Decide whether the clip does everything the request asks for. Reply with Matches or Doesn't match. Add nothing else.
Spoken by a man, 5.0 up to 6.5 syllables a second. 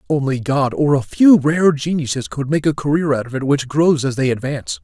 Matches